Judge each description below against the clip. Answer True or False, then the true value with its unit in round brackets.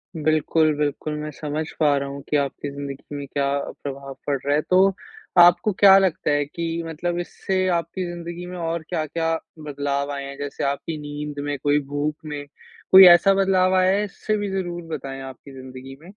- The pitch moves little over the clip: False (3.6 semitones)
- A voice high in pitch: False (155 Hz)